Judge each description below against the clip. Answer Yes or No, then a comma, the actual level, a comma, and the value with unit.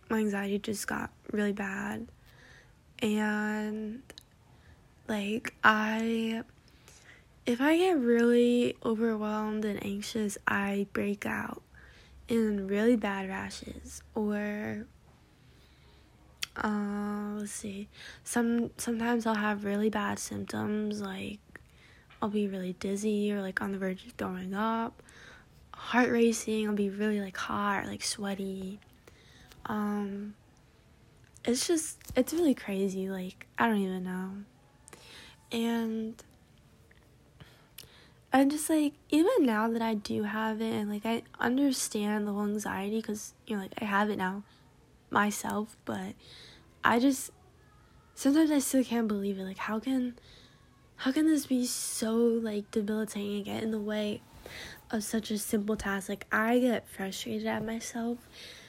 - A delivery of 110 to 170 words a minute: Yes, slow, 135 wpm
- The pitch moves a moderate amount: No, narrow, 2.3 semitones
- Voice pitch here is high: Yes, high, 215 Hz